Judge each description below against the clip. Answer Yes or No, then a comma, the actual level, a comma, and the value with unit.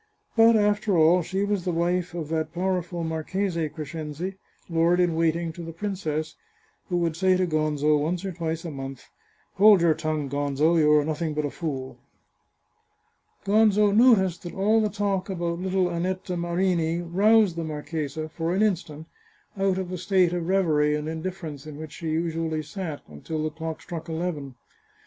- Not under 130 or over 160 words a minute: No, average, 175 wpm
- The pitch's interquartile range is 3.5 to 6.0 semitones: No, average, 3.1 semitones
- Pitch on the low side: No, medium, 170 Hz